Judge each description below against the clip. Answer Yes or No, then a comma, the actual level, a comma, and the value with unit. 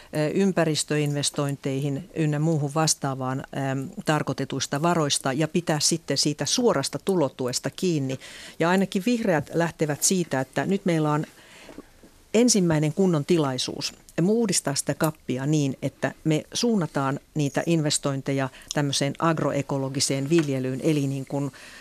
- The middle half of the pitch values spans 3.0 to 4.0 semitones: Yes, average, 3.3 semitones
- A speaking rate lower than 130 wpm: Yes, average, 115 wpm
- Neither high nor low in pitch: Yes, medium, 150 Hz